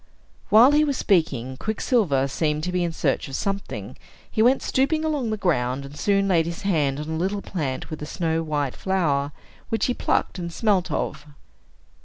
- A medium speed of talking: Yes, average, 190 wpm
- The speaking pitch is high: No, medium, 170 Hz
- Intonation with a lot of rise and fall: Yes, wide, 5.8 semitones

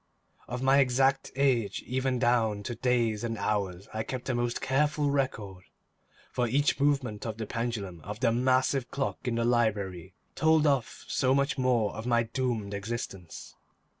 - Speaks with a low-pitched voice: Yes, low, 120 Hz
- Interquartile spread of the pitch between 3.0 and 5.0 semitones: Yes, average, 3.6 semitones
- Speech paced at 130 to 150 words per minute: No, average, 165 wpm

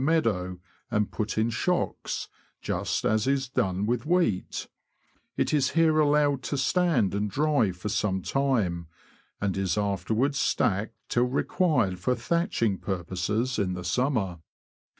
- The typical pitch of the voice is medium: No, low, 115 Hz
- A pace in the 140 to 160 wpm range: Yes, average, 145 wpm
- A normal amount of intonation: No, wide, 6.3 semitones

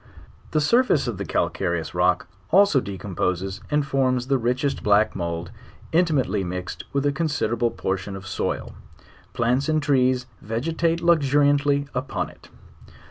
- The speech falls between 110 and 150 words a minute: Yes, slow, 135 wpm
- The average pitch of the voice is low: Yes, low, 130 Hz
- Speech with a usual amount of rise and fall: No, wide, 6.8 semitones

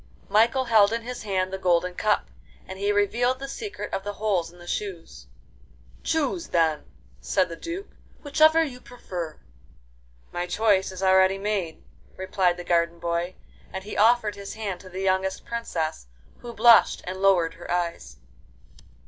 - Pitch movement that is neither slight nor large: Yes, average, 4.3 semitones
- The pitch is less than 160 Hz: No, high, 190 Hz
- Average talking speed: Yes, average, 160 wpm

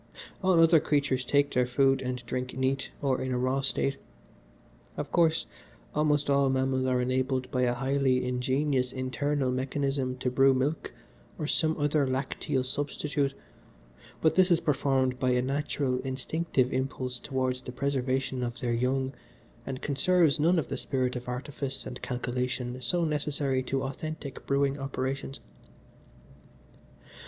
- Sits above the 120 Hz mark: Yes, low, 135 Hz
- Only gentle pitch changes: Yes, narrow, 1.9 semitones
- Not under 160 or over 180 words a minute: No, average, 145 wpm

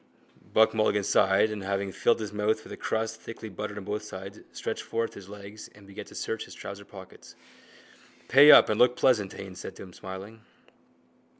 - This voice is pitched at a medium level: No, low, 105 Hz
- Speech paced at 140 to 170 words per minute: No, average, 195 wpm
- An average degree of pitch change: No, narrow, 2.0 semitones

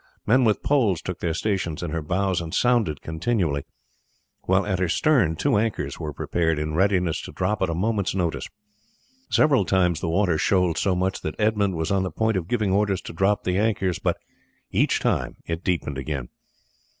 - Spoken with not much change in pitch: No, average, 3.8 semitones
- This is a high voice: No, very low, 95 Hz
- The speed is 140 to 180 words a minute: No, average, 190 wpm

